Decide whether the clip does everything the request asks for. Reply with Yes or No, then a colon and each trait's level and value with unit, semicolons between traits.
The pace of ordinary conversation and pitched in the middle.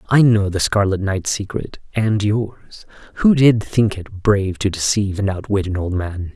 No: average, 180 wpm; low, 100 Hz